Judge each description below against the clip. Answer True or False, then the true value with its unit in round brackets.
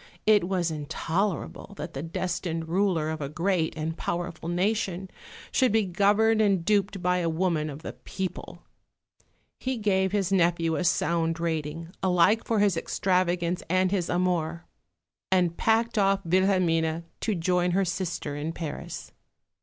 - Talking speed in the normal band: True (145 wpm)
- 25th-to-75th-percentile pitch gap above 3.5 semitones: False (2.9 semitones)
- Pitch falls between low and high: True (180 Hz)